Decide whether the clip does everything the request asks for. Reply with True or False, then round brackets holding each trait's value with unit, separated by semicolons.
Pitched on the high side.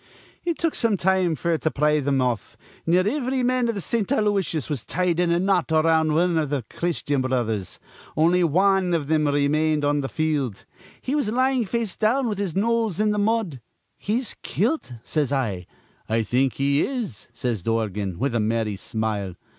False (160 Hz)